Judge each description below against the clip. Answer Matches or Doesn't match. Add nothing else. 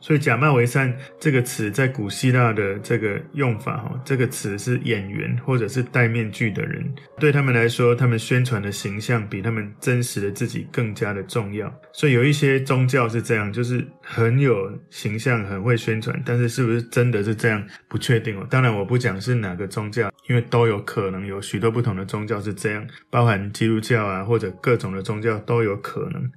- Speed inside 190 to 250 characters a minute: Doesn't match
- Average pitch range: Matches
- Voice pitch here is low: Matches